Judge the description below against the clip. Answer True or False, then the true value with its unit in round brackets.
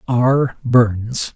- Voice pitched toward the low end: True (120 Hz)